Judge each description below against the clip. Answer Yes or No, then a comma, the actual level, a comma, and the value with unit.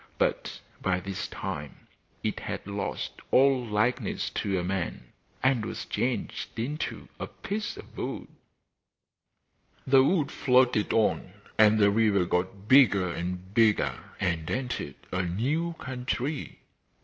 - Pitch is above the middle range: No, low, 110 Hz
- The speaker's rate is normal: No, slow, 125 wpm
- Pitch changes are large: Yes, wide, 5.7 semitones